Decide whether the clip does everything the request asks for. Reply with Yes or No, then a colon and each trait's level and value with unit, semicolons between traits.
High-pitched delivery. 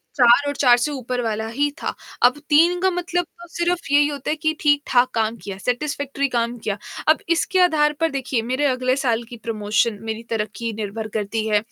Yes: very high, 255 Hz